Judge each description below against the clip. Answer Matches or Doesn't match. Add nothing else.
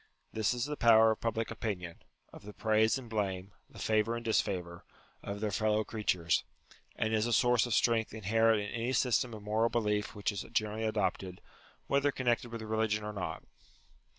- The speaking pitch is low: Matches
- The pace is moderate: Matches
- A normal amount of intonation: Doesn't match